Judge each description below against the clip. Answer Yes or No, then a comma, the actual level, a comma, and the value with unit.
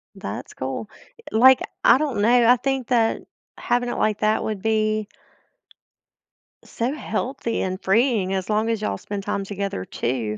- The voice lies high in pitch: Yes, high, 215 Hz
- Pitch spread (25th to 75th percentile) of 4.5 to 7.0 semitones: No, average, 3.6 semitones